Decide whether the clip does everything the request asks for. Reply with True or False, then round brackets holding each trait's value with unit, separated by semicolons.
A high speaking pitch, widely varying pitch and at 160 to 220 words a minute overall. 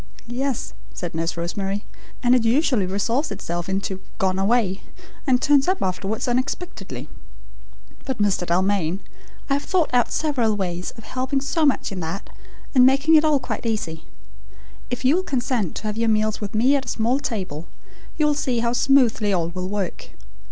True (225 Hz; 5.8 semitones; 175 wpm)